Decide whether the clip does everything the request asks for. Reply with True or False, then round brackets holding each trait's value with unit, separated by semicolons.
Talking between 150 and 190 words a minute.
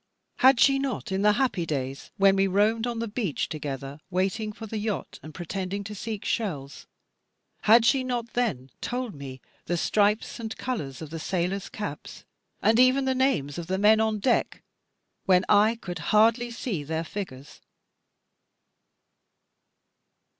True (155 wpm)